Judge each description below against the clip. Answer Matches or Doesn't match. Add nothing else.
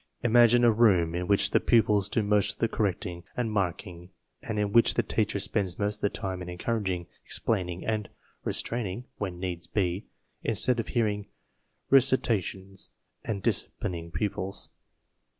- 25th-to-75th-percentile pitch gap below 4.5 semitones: Matches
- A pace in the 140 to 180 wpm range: Matches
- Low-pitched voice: Matches